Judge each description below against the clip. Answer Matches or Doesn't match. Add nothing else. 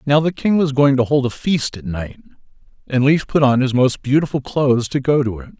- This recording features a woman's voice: Doesn't match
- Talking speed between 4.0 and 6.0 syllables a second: Matches